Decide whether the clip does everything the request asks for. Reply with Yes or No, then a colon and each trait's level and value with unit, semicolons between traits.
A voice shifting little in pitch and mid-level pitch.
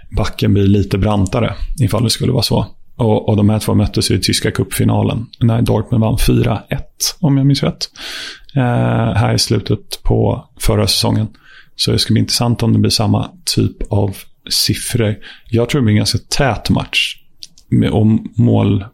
No: narrow, 2.2 semitones; low, 110 Hz